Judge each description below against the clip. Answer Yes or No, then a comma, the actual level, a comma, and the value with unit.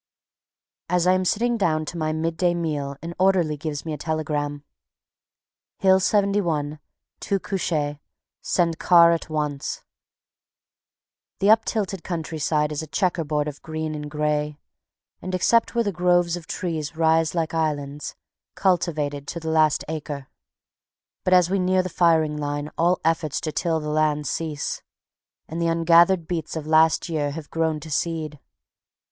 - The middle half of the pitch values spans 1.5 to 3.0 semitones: Yes, narrow, 2.6 semitones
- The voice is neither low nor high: Yes, medium, 160 Hz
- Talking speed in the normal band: Yes, average, 155 wpm